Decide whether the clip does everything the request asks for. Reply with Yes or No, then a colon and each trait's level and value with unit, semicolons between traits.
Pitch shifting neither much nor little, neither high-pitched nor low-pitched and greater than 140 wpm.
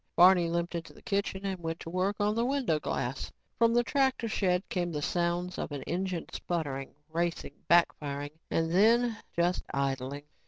Yes: average, 3.5 semitones; medium, 175 Hz; average, 170 wpm